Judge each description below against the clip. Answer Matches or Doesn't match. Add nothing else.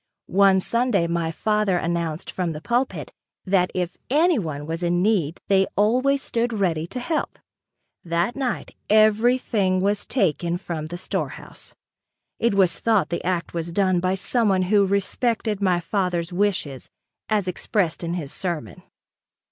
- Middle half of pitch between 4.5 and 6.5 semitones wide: Doesn't match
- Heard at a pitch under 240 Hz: Matches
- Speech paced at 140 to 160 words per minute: Matches